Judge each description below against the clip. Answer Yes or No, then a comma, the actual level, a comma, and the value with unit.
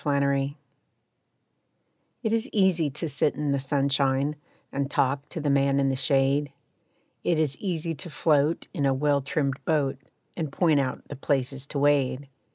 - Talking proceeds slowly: No, average, 165 wpm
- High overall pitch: No, medium, 140 Hz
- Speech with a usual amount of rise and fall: No, narrow, 1.9 semitones